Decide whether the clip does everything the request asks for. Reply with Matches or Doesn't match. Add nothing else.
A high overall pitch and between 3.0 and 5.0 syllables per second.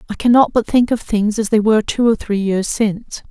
Doesn't match